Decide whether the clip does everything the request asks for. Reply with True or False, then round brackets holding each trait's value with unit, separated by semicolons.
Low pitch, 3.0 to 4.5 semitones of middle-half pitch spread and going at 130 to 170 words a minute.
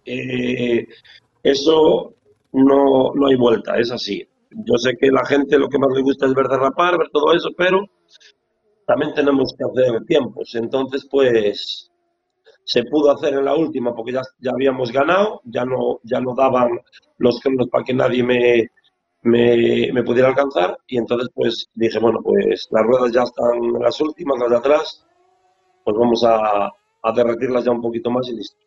False (130 Hz; 3.6 semitones; 180 wpm)